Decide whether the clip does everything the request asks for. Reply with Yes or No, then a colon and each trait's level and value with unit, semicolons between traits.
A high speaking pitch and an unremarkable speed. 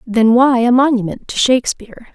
Yes: high, 240 Hz; average, 170 wpm